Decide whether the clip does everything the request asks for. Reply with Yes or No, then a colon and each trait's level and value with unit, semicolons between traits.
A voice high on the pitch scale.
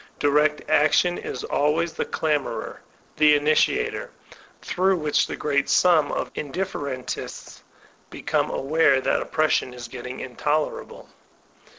No: medium, 150 Hz